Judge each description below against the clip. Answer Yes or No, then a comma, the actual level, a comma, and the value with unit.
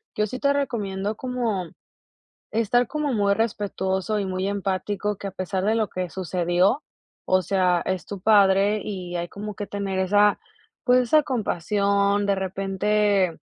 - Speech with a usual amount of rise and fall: No, narrow, 2.1 semitones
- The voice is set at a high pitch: Yes, high, 200 Hz